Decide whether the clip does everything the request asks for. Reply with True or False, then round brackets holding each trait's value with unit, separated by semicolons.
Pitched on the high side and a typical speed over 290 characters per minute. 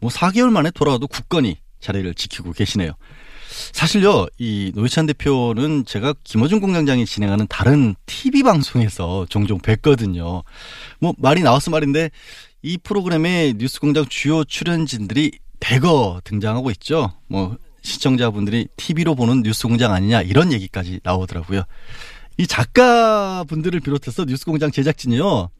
False (130 Hz; 335 characters per minute)